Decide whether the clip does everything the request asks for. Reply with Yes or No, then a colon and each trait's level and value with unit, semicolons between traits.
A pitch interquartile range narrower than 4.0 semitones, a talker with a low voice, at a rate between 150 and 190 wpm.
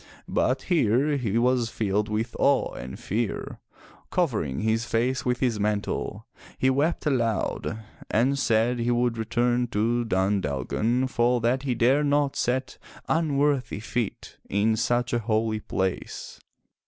No: average, 3.0 semitones; low, 120 Hz; average, 140 wpm